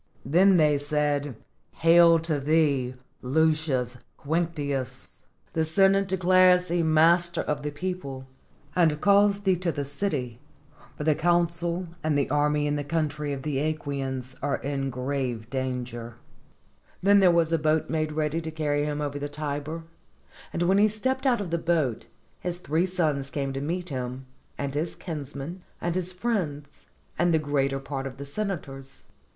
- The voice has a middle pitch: Yes, medium, 155 Hz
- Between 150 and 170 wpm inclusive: Yes, average, 160 wpm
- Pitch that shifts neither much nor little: Yes, average, 3.6 semitones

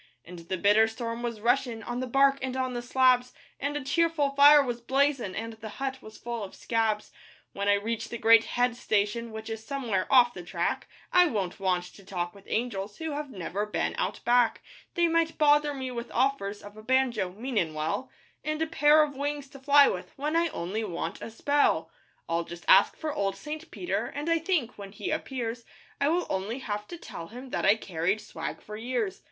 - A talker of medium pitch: No, high, 240 Hz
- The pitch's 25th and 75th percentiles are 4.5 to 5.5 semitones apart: Yes, average, 5.2 semitones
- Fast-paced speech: Yes, fast, 210 wpm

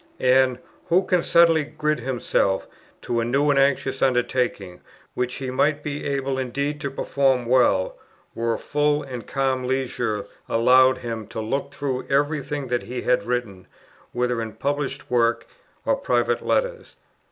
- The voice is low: Yes, low, 130 Hz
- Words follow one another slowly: No, average, 155 wpm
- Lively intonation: No, average, 2.9 semitones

